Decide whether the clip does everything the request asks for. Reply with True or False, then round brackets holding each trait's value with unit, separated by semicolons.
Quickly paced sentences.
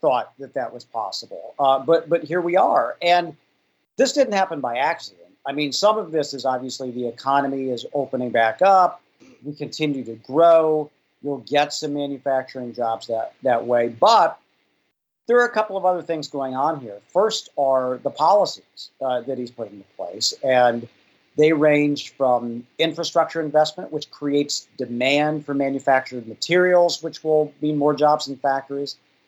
False (170 wpm)